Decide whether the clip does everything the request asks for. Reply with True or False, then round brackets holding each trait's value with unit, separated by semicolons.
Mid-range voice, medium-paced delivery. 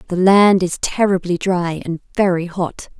True (180 Hz; 160 wpm)